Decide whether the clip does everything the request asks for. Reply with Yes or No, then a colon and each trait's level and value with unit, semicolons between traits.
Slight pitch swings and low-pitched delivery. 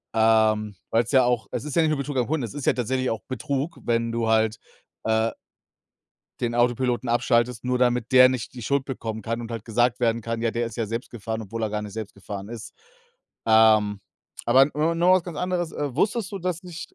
No: average, 3.3 semitones; low, 120 Hz